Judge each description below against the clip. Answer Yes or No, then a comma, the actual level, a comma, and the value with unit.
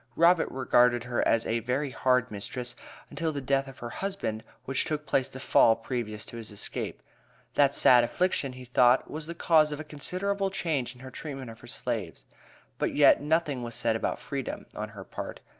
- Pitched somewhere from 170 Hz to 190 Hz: No, low, 130 Hz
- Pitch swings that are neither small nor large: Yes, average, 4.2 semitones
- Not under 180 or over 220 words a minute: Yes, average, 195 wpm